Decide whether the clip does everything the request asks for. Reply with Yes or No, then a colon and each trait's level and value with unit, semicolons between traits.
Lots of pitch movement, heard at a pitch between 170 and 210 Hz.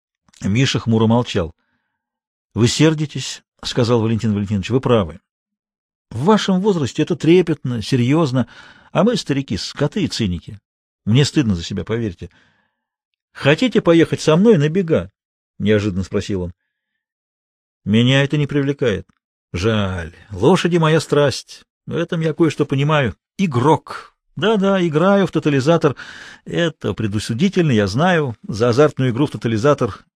No: wide, 6.5 semitones; medium, 140 Hz